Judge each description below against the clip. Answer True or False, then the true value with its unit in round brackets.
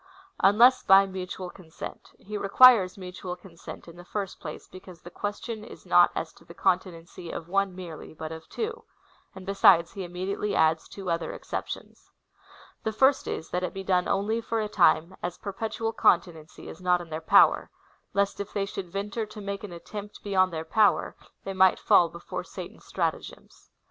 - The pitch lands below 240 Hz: True (190 Hz)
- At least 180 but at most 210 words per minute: True (185 wpm)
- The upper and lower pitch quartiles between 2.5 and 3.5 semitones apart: True (2.8 semitones)